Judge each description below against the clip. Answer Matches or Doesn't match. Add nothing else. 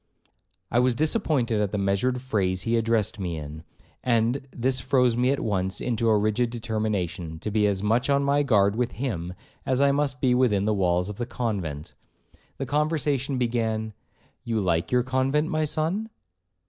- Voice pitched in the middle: Doesn't match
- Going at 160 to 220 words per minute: Matches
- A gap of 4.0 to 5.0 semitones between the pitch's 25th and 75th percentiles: Matches